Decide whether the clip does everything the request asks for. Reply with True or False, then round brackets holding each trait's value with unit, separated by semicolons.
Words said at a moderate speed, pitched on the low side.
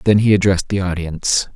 True (190 wpm; 95 Hz)